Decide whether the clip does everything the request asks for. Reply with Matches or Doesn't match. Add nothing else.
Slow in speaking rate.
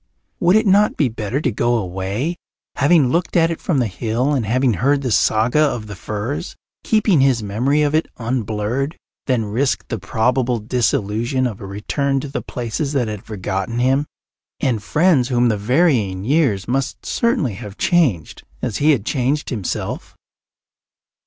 Doesn't match